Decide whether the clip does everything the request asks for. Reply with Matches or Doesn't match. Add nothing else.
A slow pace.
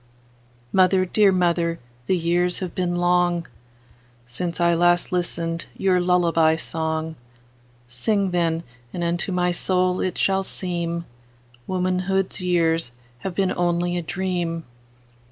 Matches